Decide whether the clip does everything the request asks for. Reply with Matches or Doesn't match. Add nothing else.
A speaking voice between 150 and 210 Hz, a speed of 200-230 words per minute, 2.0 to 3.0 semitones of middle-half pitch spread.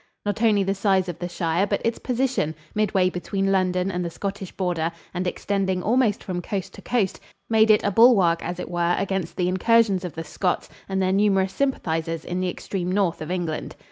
Matches